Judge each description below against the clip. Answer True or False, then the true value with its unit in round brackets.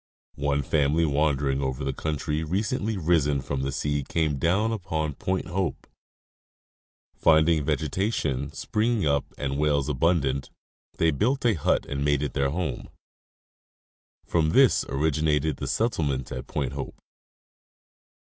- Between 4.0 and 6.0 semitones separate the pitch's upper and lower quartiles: False (3.4 semitones)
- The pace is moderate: False (130 wpm)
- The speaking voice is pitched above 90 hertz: False (75 Hz)